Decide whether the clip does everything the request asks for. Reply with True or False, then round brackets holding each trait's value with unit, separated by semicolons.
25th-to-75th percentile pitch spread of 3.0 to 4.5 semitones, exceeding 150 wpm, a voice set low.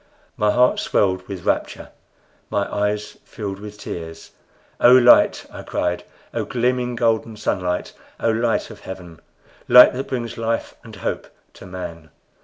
False (4.2 semitones; 145 wpm; 105 Hz)